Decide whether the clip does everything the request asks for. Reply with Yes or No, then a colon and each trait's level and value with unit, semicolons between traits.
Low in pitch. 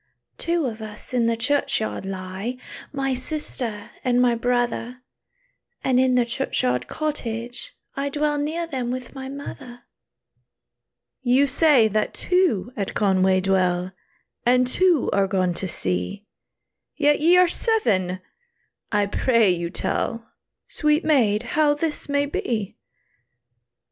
No: high, 245 Hz